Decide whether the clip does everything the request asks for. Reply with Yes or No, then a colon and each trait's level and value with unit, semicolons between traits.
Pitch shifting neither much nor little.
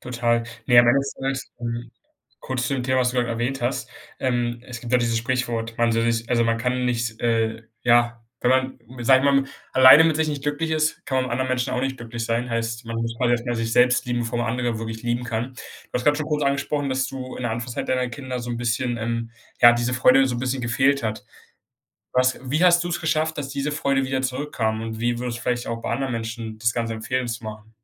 No: narrow, 2.0 semitones